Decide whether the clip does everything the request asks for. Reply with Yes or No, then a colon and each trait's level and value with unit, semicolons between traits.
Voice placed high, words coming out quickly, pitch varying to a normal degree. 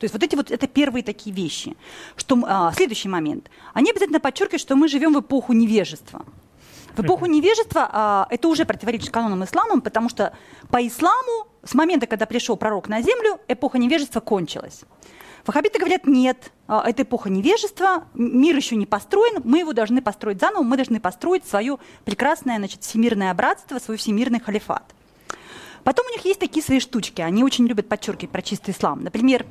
No: high, 245 Hz; fast, 175 wpm; wide, 6.7 semitones